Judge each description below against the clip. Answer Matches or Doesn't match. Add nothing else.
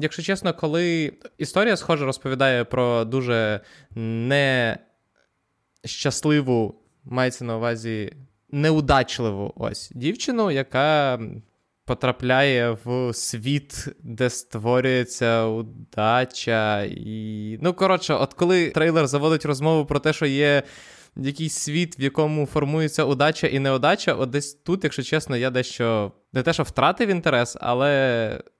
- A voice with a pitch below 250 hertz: Matches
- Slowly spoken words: Doesn't match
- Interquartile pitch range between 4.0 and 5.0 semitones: Matches